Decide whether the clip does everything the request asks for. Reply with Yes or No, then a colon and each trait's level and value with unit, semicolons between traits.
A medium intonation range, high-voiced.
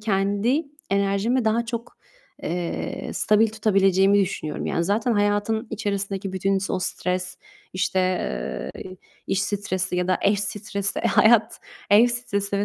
No: narrow, 2.2 semitones; high, 200 Hz